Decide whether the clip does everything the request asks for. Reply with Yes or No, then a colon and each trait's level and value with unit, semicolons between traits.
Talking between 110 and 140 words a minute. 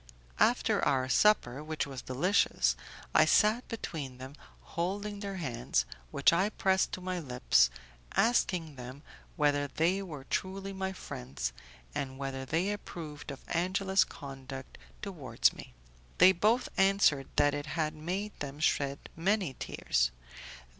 Yes: slow, 135 wpm